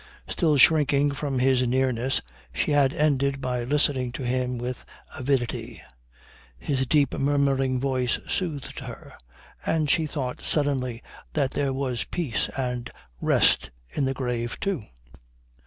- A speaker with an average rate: No, slow, 130 wpm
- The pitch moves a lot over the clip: No, narrow, 2.4 semitones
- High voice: No, low, 135 Hz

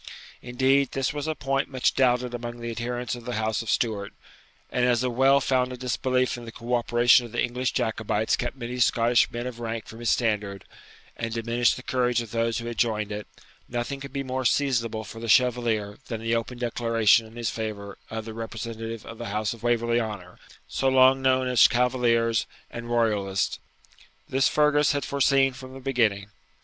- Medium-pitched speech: No, low, 120 Hz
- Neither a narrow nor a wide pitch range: No, narrow, 2.0 semitones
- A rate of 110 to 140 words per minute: No, average, 195 wpm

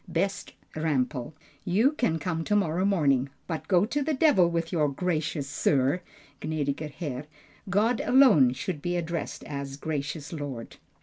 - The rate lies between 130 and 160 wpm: Yes, average, 150 wpm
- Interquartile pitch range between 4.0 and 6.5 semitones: Yes, average, 4.6 semitones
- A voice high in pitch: No, medium, 160 Hz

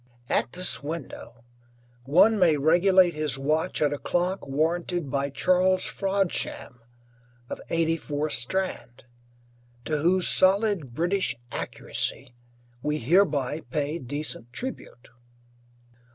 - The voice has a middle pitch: Yes, medium, 160 Hz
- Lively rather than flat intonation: No, average, 4.5 semitones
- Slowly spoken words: Yes, slow, 105 wpm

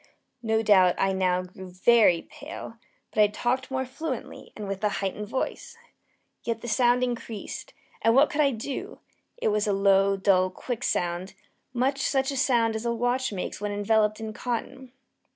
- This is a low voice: No, high, 225 Hz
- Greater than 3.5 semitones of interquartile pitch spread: Yes, average, 4.3 semitones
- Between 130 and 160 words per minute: No, average, 175 wpm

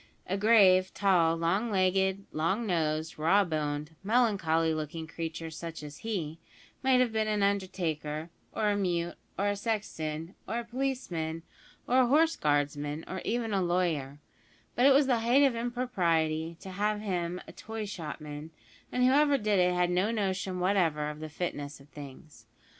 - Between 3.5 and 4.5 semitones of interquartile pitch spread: No, average, 5.2 semitones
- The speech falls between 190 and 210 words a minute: No, average, 170 wpm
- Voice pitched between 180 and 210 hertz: Yes, medium, 185 Hz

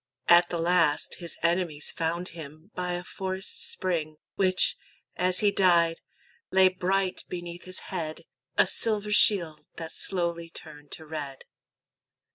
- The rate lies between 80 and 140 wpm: Yes, slow, 135 wpm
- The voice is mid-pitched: Yes, medium, 175 Hz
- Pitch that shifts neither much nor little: No, narrow, 2.3 semitones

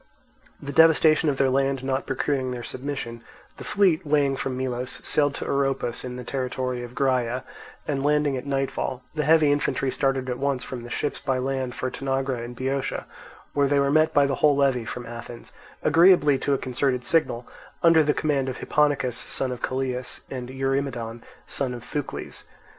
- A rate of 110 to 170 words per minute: No, average, 180 wpm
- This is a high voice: No, low, 135 Hz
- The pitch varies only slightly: Yes, narrow, 2.1 semitones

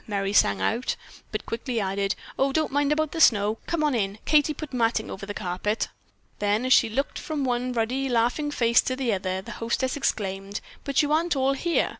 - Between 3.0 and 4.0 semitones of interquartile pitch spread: No, average, 5.3 semitones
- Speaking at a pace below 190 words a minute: No, average, 200 wpm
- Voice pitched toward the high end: Yes, high, 240 Hz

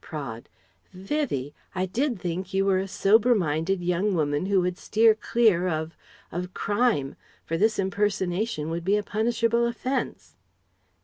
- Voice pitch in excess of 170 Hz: Yes, high, 190 Hz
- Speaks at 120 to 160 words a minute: Yes, average, 145 wpm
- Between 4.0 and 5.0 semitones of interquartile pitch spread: Yes, average, 4.6 semitones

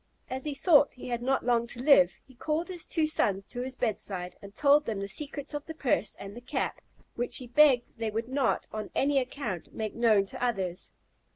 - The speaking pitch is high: Yes, high, 245 Hz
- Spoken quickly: Yes, fast, 215 wpm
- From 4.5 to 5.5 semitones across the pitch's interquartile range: Yes, average, 4.8 semitones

